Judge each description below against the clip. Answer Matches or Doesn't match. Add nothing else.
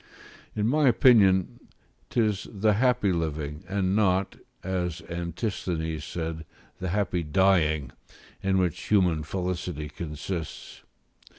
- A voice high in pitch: Doesn't match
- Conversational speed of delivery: Doesn't match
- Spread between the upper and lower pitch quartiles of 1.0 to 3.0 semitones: Doesn't match